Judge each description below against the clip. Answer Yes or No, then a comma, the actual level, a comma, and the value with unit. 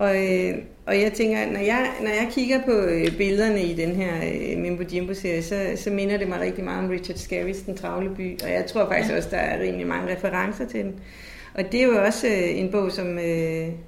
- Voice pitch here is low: No, high, 190 Hz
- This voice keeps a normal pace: No, fast, 240 wpm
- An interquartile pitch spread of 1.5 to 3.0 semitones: Yes, narrow, 2.6 semitones